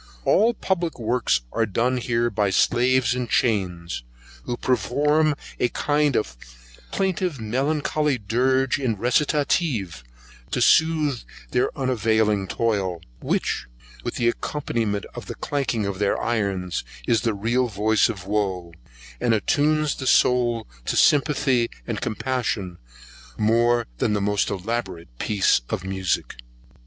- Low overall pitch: Yes, low, 115 Hz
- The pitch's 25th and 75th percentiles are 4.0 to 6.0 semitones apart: Yes, average, 4.5 semitones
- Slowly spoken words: Yes, slow, 125 wpm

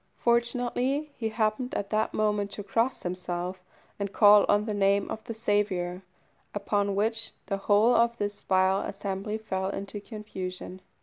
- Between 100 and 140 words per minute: No, average, 150 wpm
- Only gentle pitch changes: Yes, narrow, 2.2 semitones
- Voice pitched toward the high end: Yes, high, 205 Hz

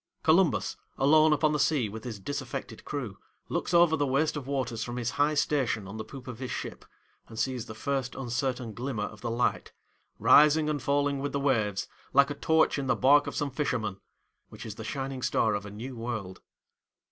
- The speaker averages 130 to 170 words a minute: No, fast, 205 wpm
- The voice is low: Yes, low, 130 Hz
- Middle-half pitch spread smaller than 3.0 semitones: No, average, 4.1 semitones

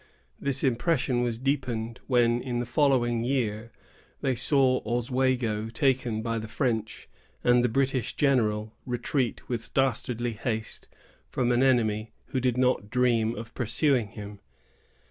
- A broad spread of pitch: No, narrow, 2.5 semitones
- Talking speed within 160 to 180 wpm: No, average, 140 wpm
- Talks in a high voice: No, low, 120 Hz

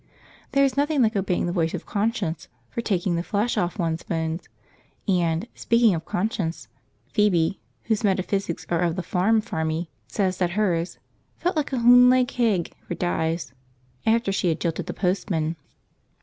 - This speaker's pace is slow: No, average, 165 wpm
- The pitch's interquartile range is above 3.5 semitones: Yes, average, 4.9 semitones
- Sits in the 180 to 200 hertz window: Yes, medium, 185 Hz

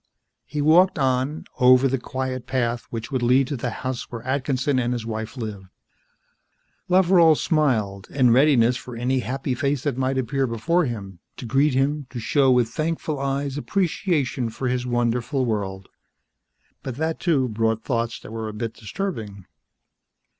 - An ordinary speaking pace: Yes, average, 160 wpm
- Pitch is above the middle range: No, low, 130 Hz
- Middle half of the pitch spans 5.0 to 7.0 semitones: No, average, 3.4 semitones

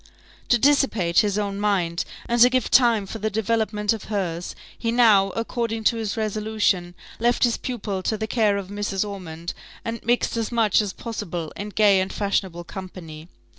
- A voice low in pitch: No, high, 210 Hz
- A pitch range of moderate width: Yes, average, 3.0 semitones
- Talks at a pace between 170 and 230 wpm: Yes, average, 175 wpm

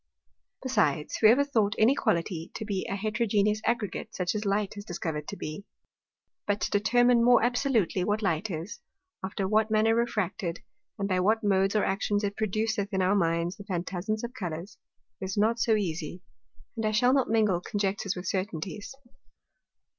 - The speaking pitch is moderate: No, high, 205 Hz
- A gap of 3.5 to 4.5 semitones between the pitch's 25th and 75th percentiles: No, average, 3.0 semitones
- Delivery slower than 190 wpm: Yes, average, 170 wpm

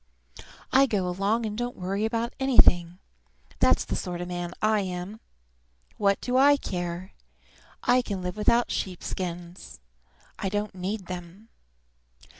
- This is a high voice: Yes, high, 195 Hz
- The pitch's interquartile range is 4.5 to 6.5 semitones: No, average, 3.8 semitones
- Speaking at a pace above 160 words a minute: No, average, 140 wpm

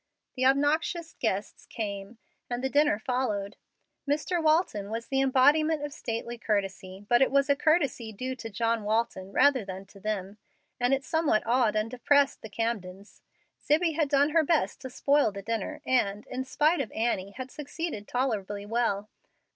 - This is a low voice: No, high, 245 Hz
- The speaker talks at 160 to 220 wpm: Yes, average, 170 wpm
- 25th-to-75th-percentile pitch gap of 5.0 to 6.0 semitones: Yes, wide, 5.4 semitones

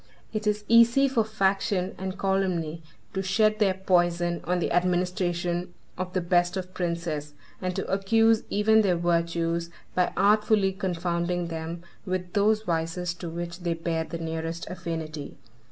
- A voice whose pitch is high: No, medium, 180 Hz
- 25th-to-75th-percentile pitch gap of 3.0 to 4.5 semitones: No, narrow, 2.4 semitones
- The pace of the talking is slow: No, average, 150 wpm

